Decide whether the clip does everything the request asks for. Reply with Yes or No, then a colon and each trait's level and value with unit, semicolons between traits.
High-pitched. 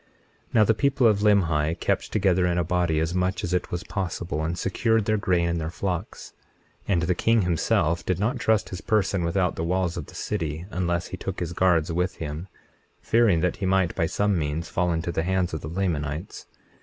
No: very low, 90 Hz